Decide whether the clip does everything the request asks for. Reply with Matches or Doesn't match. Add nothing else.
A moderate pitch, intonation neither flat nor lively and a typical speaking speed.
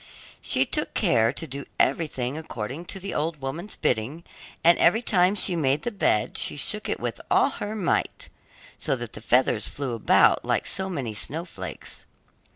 Doesn't match